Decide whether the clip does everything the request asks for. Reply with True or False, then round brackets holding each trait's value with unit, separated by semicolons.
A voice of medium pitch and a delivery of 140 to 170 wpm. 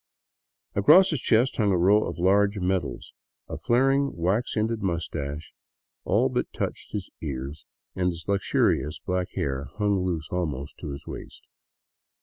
False (90 Hz; 150 wpm)